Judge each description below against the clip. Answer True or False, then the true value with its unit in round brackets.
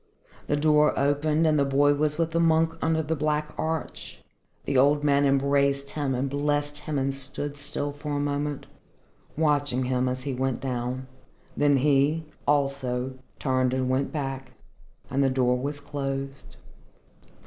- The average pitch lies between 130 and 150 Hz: True (140 Hz)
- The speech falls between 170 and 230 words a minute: False (160 wpm)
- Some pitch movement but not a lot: False (1.7 semitones)